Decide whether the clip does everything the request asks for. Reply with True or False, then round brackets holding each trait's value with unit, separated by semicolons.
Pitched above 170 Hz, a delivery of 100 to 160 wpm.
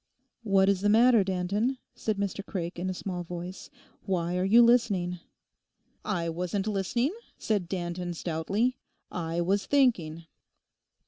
True (190 Hz; 135 wpm)